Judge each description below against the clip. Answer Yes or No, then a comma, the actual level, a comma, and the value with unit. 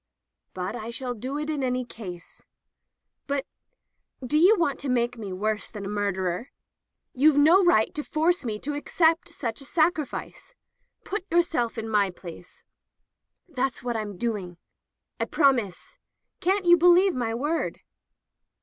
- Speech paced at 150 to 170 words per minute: Yes, average, 160 wpm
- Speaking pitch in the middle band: No, very high, 255 Hz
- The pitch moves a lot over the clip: Yes, wide, 6.4 semitones